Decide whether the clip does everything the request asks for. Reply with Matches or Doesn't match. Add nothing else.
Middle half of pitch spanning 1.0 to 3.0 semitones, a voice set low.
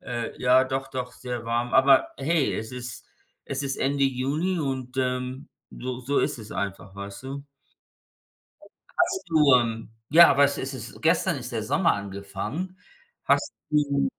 Matches